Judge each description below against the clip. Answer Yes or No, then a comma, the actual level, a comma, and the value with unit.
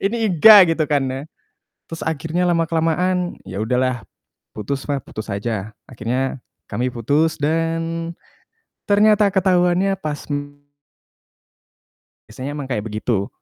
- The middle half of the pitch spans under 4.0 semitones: No, wide, 5.4 semitones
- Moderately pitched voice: Yes, medium, 150 Hz